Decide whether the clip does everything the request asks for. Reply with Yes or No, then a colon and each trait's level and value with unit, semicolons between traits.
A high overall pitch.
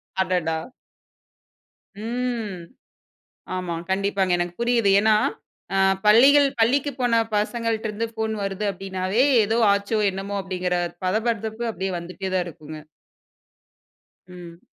Yes: high, 200 Hz